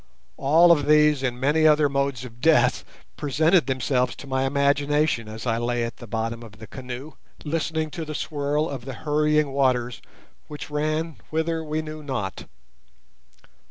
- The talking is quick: No, average, 160 wpm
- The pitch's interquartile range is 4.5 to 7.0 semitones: No, average, 3.5 semitones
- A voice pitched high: No, medium, 140 Hz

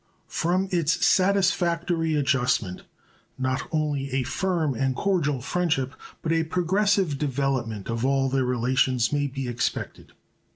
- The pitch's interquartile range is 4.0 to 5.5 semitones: Yes, average, 4.7 semitones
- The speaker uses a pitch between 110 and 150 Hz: Yes, medium, 140 Hz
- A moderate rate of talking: No, slow, 125 wpm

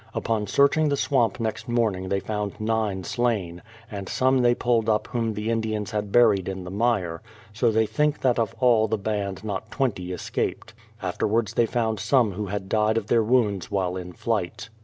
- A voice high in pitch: No, low, 110 Hz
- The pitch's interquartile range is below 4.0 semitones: Yes, average, 3.1 semitones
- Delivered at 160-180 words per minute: No, average, 195 wpm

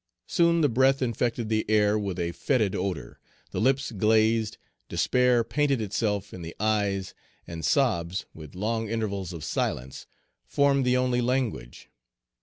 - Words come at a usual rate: Yes, average, 145 wpm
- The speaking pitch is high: No, low, 110 Hz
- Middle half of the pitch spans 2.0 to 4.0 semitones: No, average, 4.5 semitones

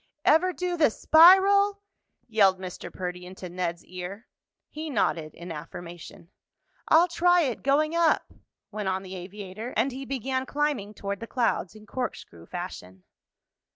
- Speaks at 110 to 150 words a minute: Yes, average, 145 wpm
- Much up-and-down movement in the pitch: Yes, wide, 8.9 semitones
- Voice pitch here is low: No, high, 215 Hz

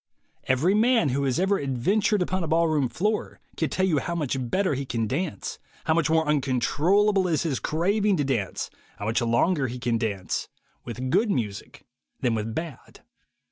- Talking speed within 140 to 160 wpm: No, average, 180 wpm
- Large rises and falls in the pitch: Yes, wide, 6.9 semitones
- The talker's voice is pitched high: No, medium, 150 Hz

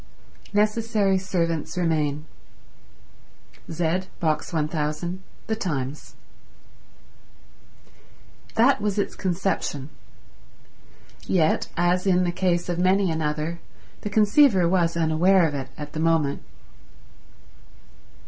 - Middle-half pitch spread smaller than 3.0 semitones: No, average, 3.5 semitones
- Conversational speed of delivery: No, slow, 95 wpm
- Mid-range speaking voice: Yes, medium, 175 Hz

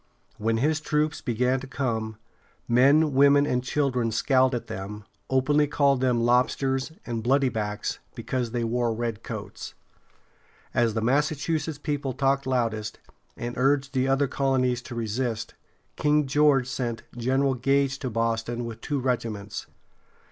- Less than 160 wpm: Yes, average, 140 wpm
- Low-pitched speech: Yes, low, 130 Hz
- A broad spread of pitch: No, average, 3.0 semitones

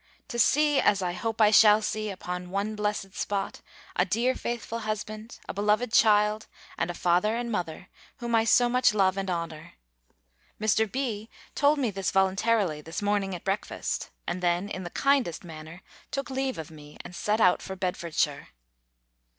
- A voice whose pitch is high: Yes, high, 205 Hz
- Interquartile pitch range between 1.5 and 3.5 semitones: No, average, 3.9 semitones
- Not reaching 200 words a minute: Yes, average, 175 wpm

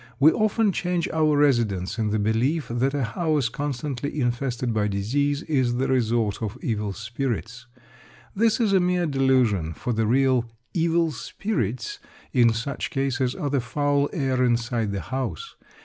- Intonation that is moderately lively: Yes, average, 4.2 semitones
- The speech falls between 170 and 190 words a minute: No, average, 155 wpm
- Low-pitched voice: Yes, low, 130 Hz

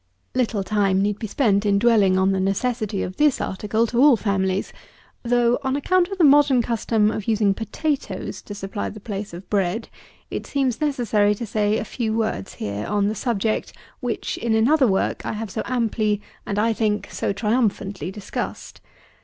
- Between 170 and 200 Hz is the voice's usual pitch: No, high, 215 Hz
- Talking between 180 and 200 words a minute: Yes, average, 185 wpm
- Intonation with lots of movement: No, average, 3.2 semitones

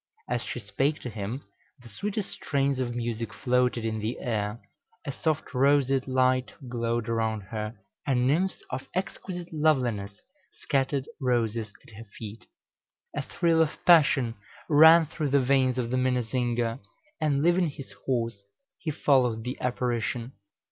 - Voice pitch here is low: Yes, low, 125 Hz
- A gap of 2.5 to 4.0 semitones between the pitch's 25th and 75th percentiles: Yes, average, 3.5 semitones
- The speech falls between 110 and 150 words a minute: Yes, average, 145 wpm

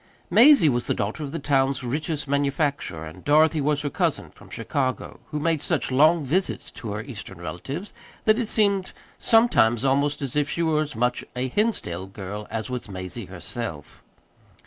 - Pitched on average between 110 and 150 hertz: Yes, medium, 140 Hz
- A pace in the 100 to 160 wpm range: No, average, 180 wpm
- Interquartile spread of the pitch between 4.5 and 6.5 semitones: Yes, wide, 5.5 semitones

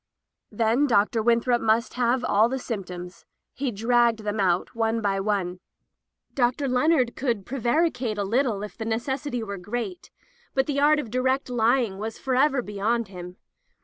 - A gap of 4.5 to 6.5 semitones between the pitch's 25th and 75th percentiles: No, average, 3.8 semitones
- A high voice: Yes, high, 230 Hz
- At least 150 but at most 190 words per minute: Yes, average, 165 wpm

